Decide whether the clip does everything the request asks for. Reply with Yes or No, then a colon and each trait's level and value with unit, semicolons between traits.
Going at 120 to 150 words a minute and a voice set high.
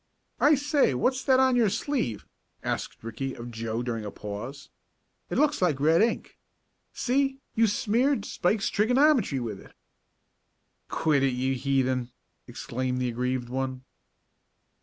No: average, 140 wpm; medium, 140 Hz